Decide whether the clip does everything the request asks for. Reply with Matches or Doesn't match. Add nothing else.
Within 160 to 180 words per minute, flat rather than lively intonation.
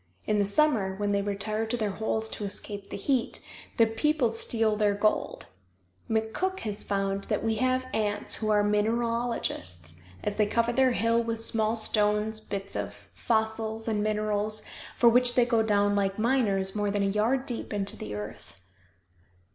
Matches